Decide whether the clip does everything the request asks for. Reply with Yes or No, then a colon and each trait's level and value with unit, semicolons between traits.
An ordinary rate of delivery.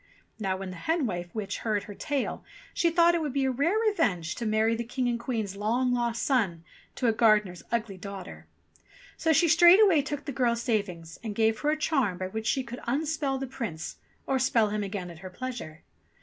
No: fast, 215 wpm